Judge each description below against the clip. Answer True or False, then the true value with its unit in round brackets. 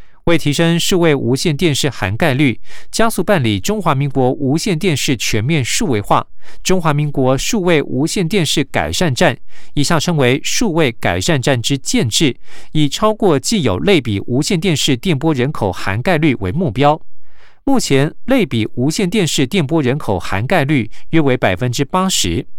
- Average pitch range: False (5.7 semitones)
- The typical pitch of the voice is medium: True (150 Hz)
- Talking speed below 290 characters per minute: True (260 characters per minute)